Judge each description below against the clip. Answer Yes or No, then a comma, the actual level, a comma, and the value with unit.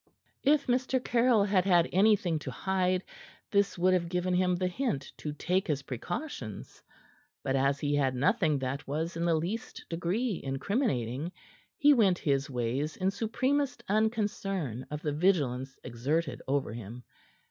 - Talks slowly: No, average, 155 wpm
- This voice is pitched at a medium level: Yes, medium, 175 Hz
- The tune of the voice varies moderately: No, wide, 6.6 semitones